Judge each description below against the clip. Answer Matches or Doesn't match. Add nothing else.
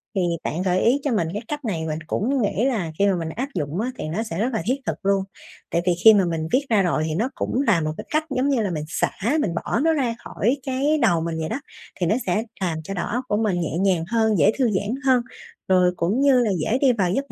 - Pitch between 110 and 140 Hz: Doesn't match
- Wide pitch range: Matches